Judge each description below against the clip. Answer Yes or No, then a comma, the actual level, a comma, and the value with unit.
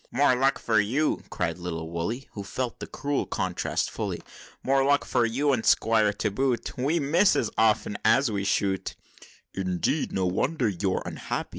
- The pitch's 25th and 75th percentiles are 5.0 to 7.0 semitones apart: Yes, wide, 5.4 semitones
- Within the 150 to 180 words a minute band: Yes, average, 170 wpm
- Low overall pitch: Yes, low, 115 Hz